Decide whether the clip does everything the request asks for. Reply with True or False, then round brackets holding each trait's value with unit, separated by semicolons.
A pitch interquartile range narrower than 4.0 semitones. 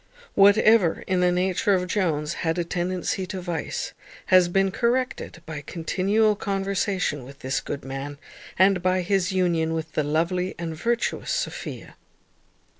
True (3.1 semitones)